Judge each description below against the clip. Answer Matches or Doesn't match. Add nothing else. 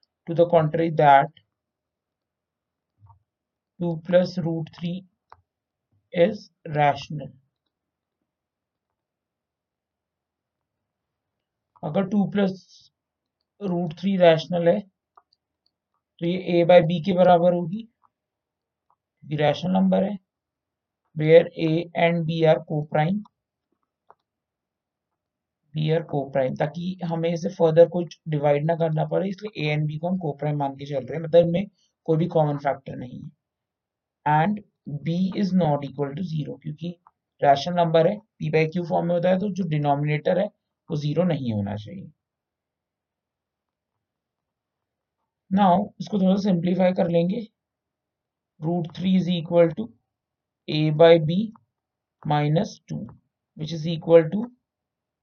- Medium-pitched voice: Matches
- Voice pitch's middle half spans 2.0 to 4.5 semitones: Matches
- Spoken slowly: Matches